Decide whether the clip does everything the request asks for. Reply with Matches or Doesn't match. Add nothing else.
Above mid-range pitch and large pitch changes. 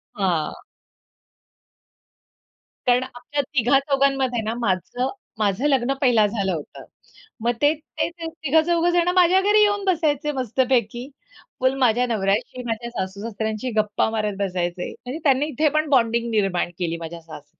Matches